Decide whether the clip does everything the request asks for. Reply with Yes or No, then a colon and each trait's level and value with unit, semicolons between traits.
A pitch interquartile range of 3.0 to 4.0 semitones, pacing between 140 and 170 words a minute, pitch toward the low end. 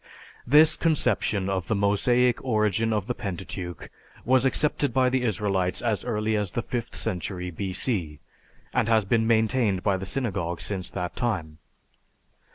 No: average, 4.4 semitones; average, 150 wpm; low, 105 Hz